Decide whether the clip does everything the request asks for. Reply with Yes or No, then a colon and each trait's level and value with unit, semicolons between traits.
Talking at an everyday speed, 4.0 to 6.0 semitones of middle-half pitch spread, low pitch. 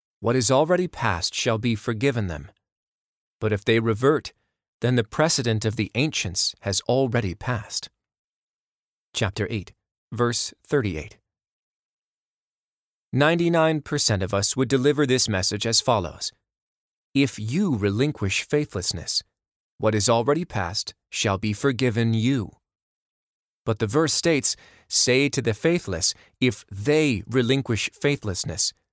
No: slow, 125 wpm; average, 4.7 semitones; low, 115 Hz